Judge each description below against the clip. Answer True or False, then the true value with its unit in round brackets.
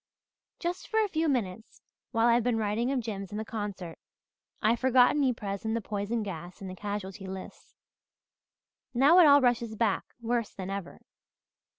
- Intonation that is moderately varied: True (3.8 semitones)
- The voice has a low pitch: False (225 Hz)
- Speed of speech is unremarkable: True (170 wpm)